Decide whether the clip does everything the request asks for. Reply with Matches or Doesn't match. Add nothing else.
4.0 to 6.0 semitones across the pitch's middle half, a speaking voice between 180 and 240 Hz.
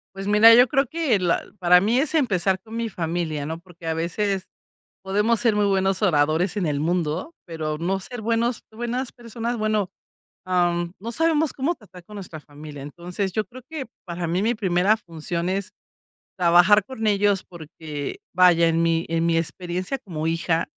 Matches